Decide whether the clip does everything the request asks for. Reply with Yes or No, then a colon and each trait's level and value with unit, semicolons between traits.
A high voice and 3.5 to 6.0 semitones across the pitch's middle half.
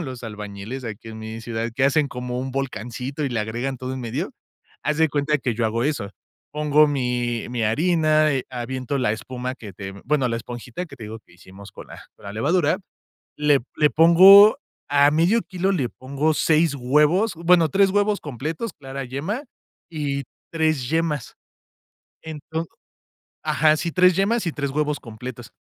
No: medium, 140 Hz; average, 4.7 semitones